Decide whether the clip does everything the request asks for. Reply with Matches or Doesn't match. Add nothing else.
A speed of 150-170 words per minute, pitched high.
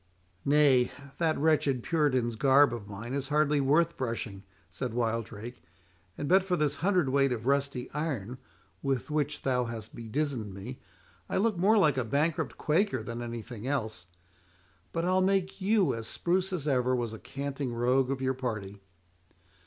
Doesn't match